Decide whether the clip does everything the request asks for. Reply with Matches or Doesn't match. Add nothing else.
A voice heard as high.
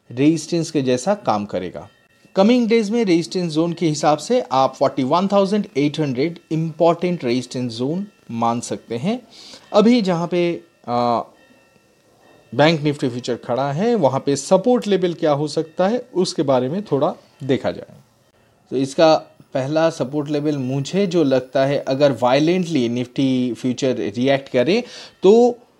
Doesn't match